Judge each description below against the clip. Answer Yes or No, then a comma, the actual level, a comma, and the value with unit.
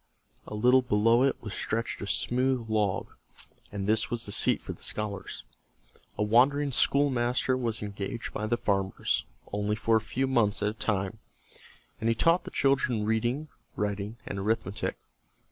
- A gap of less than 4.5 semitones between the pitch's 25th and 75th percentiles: Yes, average, 3.1 semitones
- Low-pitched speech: Yes, low, 110 Hz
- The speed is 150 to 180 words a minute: Yes, average, 160 wpm